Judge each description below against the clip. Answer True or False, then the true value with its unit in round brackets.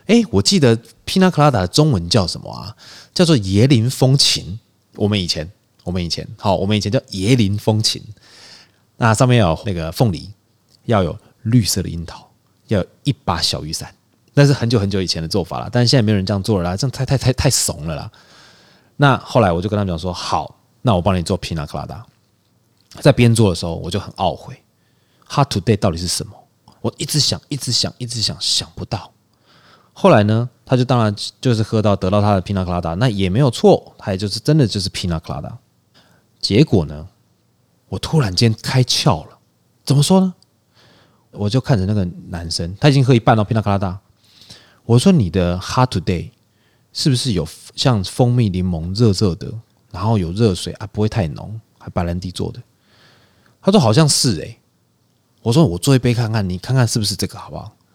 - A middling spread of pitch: True (4.6 semitones)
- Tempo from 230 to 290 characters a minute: False (300 characters per minute)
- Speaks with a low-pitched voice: True (110 Hz)